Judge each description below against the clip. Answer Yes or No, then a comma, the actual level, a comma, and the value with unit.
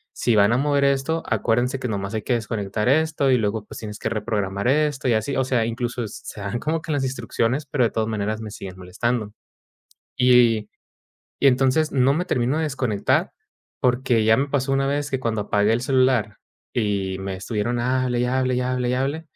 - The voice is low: Yes, low, 125 Hz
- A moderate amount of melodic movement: Yes, average, 3.6 semitones